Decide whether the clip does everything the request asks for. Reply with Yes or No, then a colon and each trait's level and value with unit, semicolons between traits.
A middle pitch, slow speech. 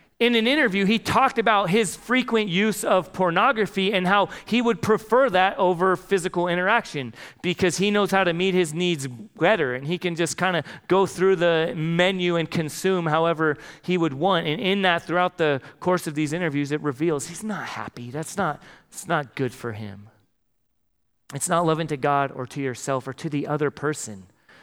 No: medium, 175 Hz; average, 190 wpm